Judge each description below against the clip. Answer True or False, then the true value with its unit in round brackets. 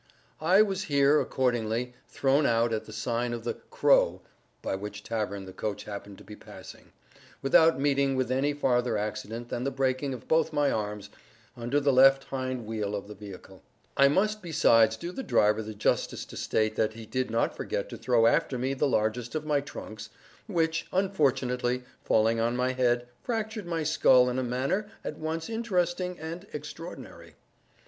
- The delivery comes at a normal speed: True (180 wpm)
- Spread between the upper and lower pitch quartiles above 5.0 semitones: True (5.4 semitones)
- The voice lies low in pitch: True (130 Hz)